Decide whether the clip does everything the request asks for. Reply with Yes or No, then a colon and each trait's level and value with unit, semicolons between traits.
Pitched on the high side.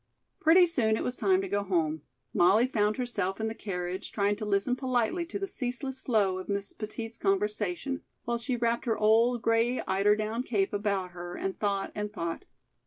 Yes: high, 215 Hz